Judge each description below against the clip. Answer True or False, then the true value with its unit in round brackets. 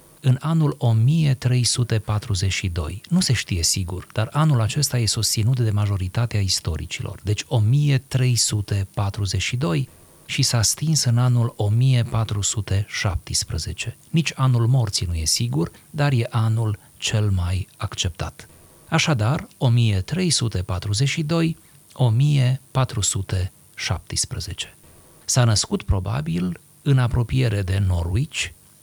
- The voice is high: False (115 Hz)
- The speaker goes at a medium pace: False (90 wpm)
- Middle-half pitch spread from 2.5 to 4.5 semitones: False (5.0 semitones)